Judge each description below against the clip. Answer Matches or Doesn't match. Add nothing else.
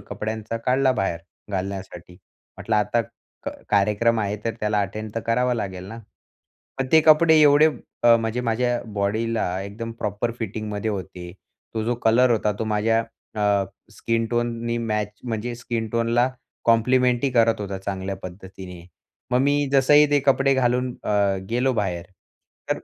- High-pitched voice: Doesn't match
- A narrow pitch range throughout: Doesn't match